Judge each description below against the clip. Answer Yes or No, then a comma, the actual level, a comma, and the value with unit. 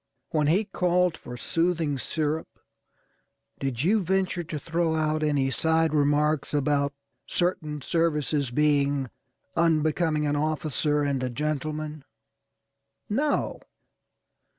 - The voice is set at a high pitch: No, medium, 155 Hz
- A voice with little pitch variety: Yes, narrow, 2.3 semitones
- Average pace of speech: No, slow, 105 wpm